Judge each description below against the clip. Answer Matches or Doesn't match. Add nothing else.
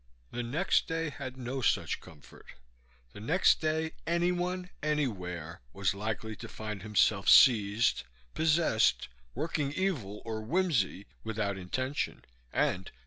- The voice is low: Matches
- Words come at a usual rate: Doesn't match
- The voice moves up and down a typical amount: Doesn't match